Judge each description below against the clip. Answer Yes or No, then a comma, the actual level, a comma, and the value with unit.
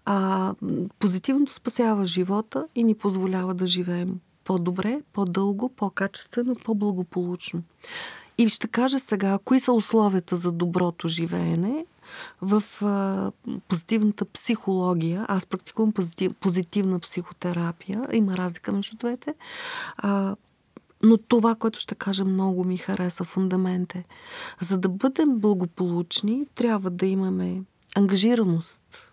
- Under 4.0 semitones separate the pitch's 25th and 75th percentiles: Yes, average, 3.6 semitones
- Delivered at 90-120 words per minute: Yes, slow, 115 wpm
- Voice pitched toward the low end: No, high, 195 Hz